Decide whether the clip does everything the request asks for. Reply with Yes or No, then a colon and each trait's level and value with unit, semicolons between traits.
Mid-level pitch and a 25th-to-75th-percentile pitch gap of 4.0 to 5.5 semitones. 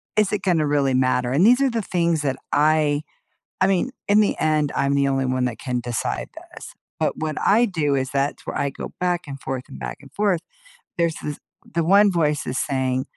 Yes: medium, 150 Hz; average, 5.0 semitones